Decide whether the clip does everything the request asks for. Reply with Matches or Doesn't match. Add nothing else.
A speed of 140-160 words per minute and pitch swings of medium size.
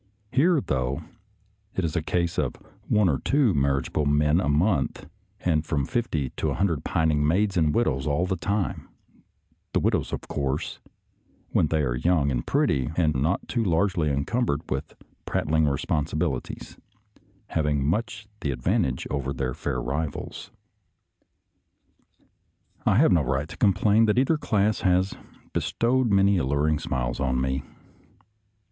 Doesn't match